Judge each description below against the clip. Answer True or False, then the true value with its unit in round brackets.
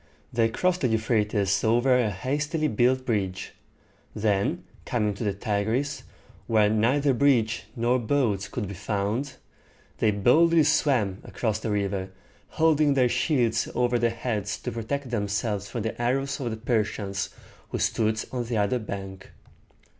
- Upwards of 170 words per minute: False (150 wpm)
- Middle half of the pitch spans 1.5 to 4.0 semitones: True (3.7 semitones)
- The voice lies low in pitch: True (115 Hz)